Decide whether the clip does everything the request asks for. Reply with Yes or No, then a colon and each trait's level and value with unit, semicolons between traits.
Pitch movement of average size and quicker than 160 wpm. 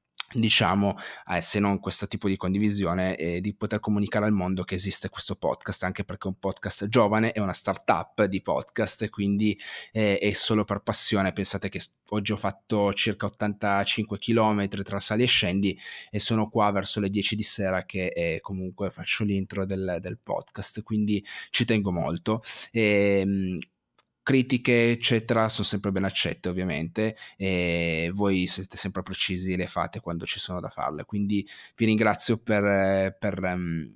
No: narrow, 2.2 semitones; fast, 170 wpm